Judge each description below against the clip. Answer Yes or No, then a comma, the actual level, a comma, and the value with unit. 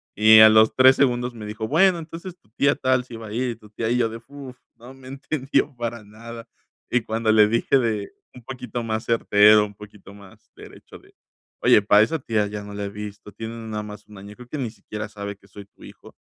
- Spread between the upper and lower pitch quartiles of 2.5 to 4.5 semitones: Yes, average, 2.9 semitones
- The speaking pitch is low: Yes, low, 110 Hz